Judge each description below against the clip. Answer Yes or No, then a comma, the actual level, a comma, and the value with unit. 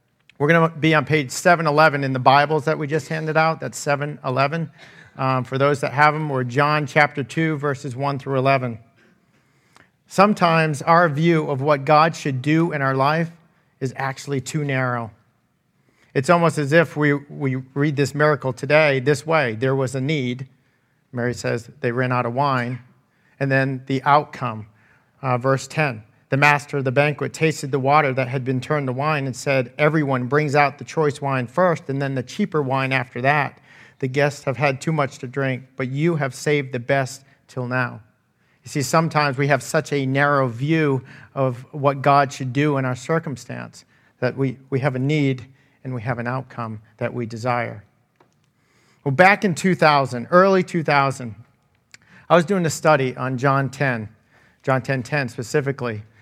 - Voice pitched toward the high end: No, medium, 140 Hz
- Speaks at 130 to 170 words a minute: No, average, 185 wpm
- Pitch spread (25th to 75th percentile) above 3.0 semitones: No, average, 2.7 semitones